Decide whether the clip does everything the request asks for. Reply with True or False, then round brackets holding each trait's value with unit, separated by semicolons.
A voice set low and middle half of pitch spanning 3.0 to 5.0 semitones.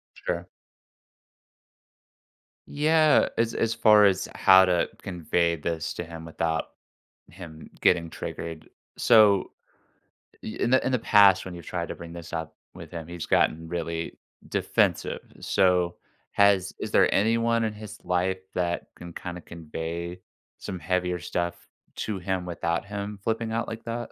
True (90 Hz; 3.8 semitones)